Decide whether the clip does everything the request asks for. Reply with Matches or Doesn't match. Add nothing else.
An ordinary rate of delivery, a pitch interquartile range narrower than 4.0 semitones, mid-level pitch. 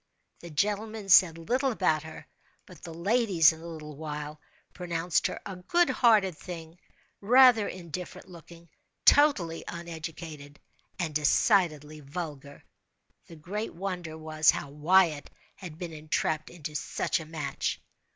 Doesn't match